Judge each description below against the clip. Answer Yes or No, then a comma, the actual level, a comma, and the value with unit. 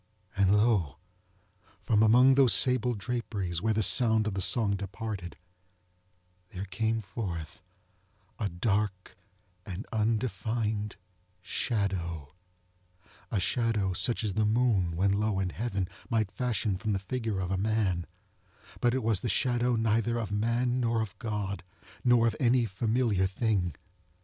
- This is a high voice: No, low, 110 Hz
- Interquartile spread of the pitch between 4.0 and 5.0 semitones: No, average, 3.3 semitones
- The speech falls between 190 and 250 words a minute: No, slow, 135 wpm